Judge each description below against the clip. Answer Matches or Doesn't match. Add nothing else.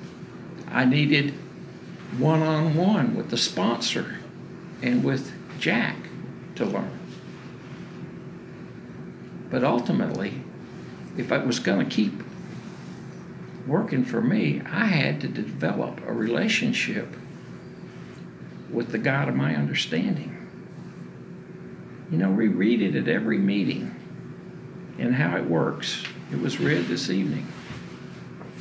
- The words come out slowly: Matches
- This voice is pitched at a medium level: Matches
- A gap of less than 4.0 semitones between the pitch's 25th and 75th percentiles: Doesn't match